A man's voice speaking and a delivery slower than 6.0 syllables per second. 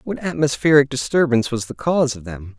No: male; 6.1 syllables/s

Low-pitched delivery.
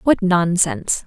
No: high, 190 Hz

